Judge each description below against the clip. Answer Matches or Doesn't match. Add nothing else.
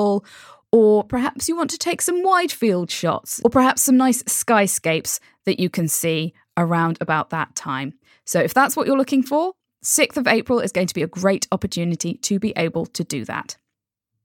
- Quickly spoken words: Doesn't match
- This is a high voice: Matches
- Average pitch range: Doesn't match